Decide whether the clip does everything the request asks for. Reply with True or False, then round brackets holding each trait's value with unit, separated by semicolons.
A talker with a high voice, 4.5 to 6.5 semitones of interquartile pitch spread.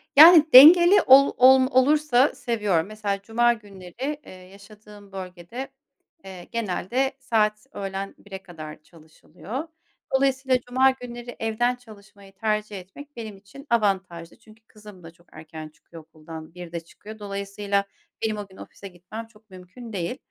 True (210 Hz; 4.9 semitones)